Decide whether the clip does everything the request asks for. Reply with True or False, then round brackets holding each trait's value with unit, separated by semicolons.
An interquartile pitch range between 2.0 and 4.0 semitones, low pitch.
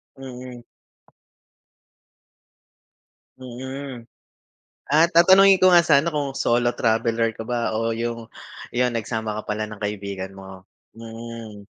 True (3.0 semitones; 115 Hz)